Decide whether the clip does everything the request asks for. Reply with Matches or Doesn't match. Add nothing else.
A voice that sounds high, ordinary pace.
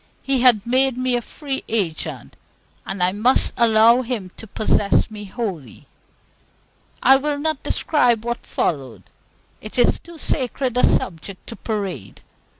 Matches